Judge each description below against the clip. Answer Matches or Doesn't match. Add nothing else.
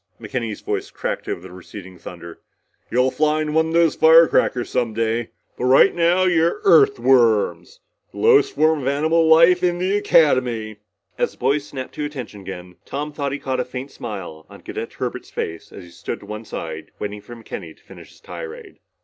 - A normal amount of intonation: Doesn't match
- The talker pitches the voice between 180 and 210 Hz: Doesn't match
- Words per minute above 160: Matches